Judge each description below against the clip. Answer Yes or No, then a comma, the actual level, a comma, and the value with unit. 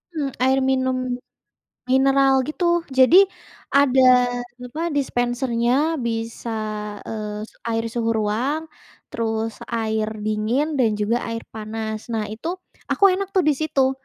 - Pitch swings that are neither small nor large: Yes, average, 3.5 semitones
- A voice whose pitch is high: Yes, high, 245 Hz